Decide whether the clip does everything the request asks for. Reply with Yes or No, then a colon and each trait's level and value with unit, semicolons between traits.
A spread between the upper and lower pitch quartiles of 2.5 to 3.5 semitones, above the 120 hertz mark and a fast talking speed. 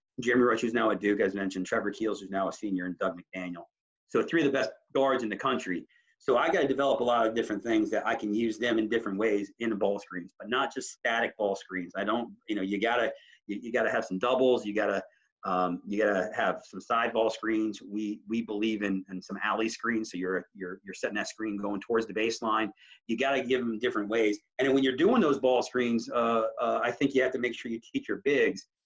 No: average, 3.2 semitones; low, 110 Hz; fast, 250 wpm